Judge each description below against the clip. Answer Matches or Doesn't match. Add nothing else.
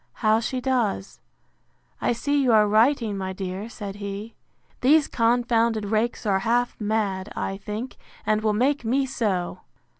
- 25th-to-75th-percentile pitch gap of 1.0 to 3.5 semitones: Matches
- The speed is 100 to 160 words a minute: Matches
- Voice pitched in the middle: Doesn't match